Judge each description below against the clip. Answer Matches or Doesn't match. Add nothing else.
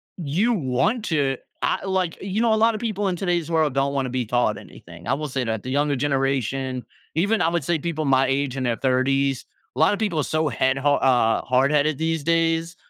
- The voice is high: Doesn't match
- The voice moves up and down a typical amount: Matches